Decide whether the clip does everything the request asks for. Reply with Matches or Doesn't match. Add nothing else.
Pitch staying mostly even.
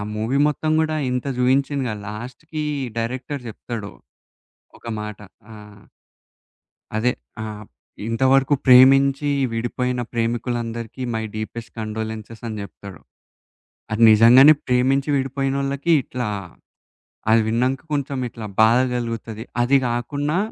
Doesn't match